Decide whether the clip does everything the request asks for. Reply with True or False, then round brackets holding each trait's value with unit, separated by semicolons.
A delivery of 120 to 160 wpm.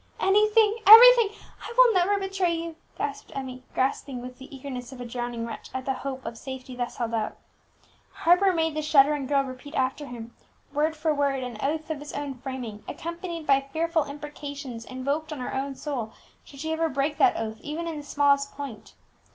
False (190 wpm)